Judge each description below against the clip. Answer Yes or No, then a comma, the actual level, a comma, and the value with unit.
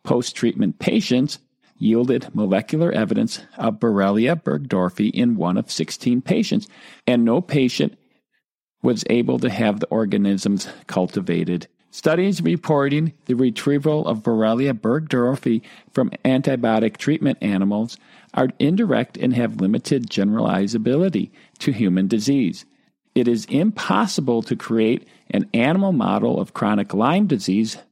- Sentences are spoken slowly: Yes, slow, 120 wpm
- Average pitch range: No, wide, 6.0 semitones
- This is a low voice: Yes, low, 130 Hz